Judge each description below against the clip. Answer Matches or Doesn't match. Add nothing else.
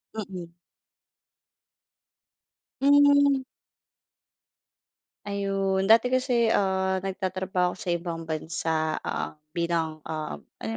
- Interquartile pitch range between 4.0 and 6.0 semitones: Matches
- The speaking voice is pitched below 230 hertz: Matches